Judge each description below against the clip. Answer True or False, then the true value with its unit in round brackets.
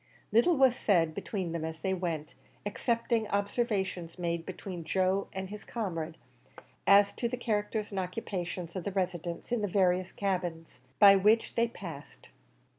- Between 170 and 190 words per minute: False (155 wpm)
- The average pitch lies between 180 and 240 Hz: True (190 Hz)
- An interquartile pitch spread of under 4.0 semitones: True (3.3 semitones)